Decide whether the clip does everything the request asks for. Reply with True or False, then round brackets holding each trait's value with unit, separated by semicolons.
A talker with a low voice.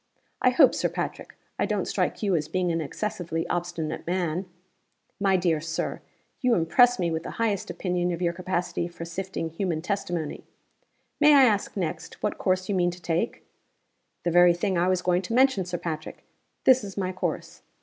False (180 Hz)